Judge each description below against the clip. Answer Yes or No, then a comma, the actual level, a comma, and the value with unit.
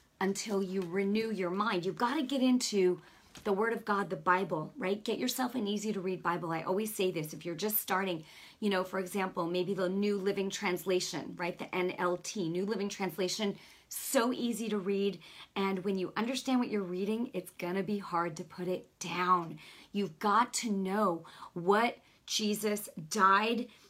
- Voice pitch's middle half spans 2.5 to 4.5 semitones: Yes, average, 2.8 semitones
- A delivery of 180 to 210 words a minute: Yes, average, 185 wpm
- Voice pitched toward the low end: No, high, 195 Hz